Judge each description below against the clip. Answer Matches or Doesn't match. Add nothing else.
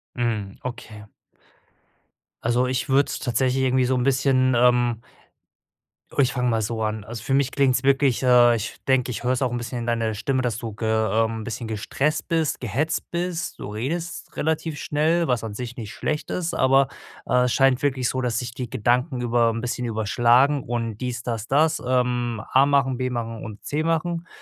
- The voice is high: Doesn't match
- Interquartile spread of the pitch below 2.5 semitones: Doesn't match